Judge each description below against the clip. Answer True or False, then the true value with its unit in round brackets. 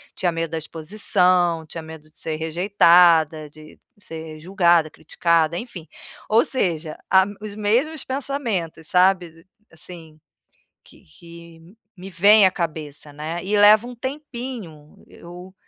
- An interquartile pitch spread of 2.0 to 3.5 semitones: False (4.1 semitones)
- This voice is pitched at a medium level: True (170 Hz)